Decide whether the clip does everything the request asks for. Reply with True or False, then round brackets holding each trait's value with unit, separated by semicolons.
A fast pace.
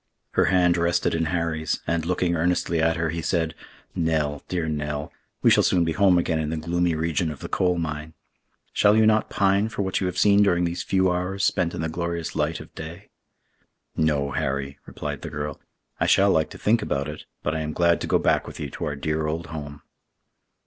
True (220 wpm)